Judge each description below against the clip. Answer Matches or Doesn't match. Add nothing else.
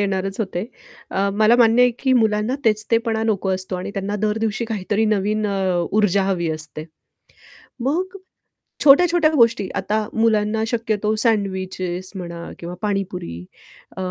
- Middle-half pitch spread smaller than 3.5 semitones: Matches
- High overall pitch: Matches